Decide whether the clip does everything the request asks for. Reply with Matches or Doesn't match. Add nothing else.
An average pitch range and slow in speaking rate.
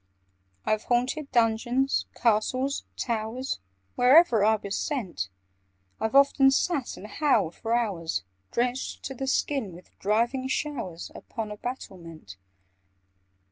Matches